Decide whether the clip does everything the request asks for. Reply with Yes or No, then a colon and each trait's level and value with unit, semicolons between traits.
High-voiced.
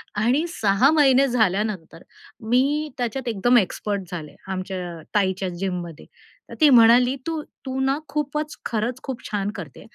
Yes: high, 230 Hz